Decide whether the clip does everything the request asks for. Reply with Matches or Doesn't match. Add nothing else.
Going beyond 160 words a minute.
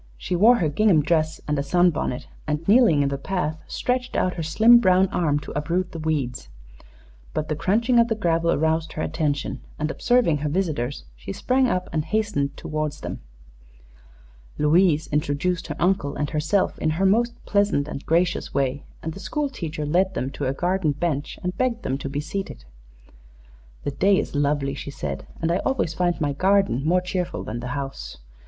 Matches